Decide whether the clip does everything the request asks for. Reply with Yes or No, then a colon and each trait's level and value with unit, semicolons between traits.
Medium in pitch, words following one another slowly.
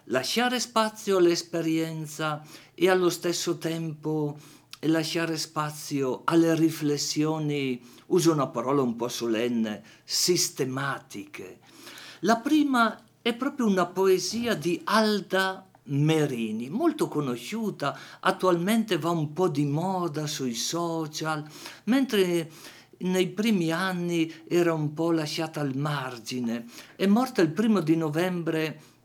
Yes: medium, 165 Hz; slow, 110 wpm